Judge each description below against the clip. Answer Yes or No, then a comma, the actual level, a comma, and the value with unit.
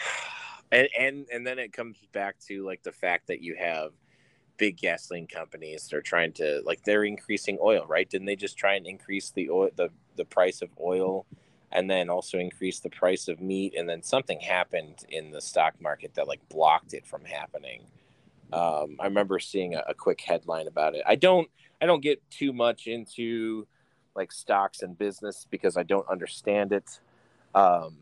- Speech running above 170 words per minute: Yes, average, 190 wpm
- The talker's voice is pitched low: Yes, low, 100 Hz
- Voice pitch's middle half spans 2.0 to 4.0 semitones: No, average, 4.5 semitones